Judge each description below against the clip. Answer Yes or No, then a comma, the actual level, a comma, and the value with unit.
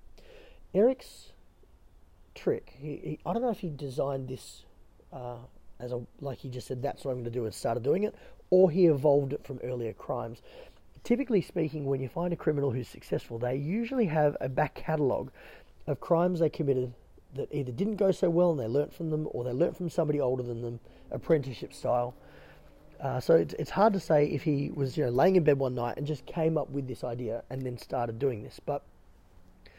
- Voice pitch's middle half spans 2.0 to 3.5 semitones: No, average, 5.2 semitones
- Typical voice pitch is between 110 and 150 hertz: Yes, medium, 140 Hz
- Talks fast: Yes, fast, 210 wpm